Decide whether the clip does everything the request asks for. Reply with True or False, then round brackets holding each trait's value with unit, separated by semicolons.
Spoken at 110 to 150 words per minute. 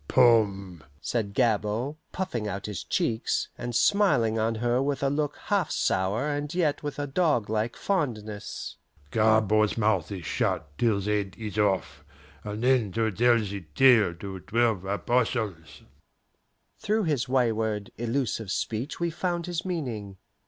True (145 wpm)